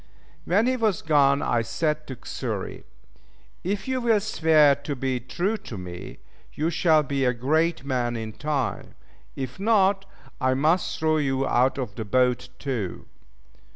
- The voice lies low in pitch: No, medium, 145 Hz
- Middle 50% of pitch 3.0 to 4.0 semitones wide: No, average, 4.9 semitones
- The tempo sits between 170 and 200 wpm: No, average, 155 wpm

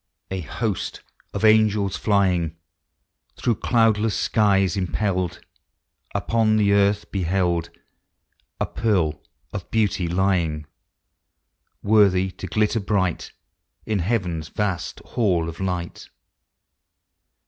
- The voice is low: Yes, very low, 95 Hz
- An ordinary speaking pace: No, slow, 95 wpm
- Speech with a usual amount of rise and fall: Yes, average, 3.2 semitones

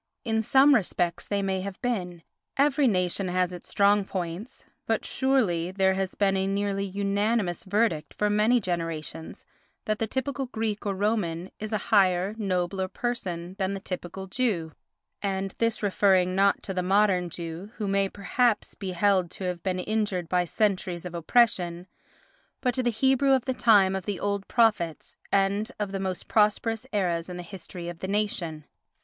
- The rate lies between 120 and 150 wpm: No, average, 165 wpm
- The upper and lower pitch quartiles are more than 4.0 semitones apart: No, average, 3.0 semitones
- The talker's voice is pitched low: No, high, 195 Hz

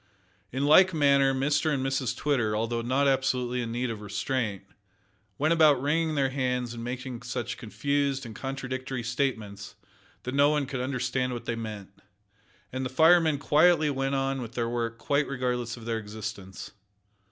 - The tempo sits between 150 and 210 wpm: Yes, average, 165 wpm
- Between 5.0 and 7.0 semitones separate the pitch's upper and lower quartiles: No, average, 3.1 semitones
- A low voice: Yes, low, 130 Hz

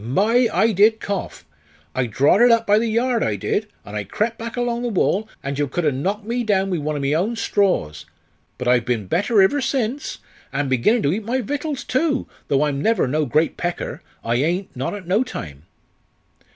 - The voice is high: Yes, high, 195 Hz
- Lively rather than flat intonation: Yes, wide, 8.7 semitones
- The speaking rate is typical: No, fast, 210 wpm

